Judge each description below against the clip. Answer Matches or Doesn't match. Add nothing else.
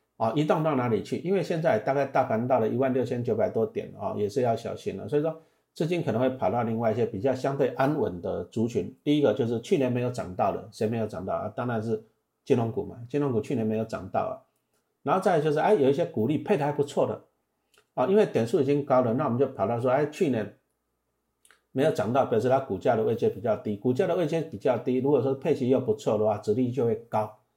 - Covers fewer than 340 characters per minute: Doesn't match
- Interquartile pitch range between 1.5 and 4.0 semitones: Doesn't match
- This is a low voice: Matches